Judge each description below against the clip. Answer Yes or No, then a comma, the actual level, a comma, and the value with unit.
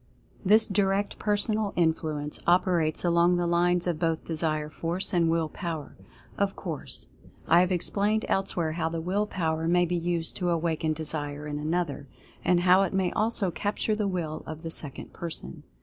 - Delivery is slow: No, average, 170 wpm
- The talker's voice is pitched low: No, medium, 170 Hz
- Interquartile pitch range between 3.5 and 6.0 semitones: No, average, 3.0 semitones